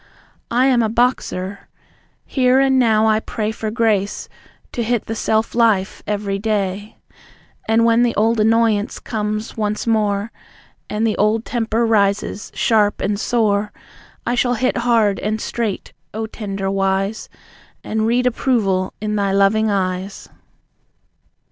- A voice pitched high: Yes, high, 215 Hz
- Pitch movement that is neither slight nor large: No, narrow, 2.2 semitones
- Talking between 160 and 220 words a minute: No, average, 140 wpm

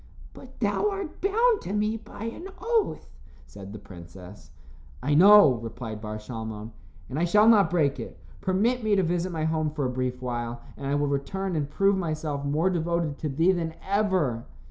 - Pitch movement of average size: No, wide, 7.6 semitones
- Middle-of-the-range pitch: Yes, medium, 160 Hz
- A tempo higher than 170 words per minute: Yes, average, 190 wpm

